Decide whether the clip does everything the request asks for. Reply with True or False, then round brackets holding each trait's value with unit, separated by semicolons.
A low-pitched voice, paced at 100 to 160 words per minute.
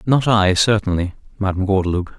True (100 Hz; 140 wpm)